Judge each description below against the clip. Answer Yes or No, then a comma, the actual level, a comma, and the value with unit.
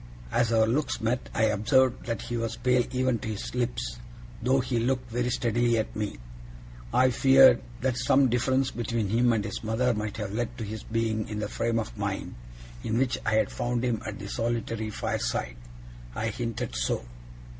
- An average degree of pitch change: No, narrow, 2.2 semitones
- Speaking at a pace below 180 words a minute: No, average, 190 wpm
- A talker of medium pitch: No, low, 115 Hz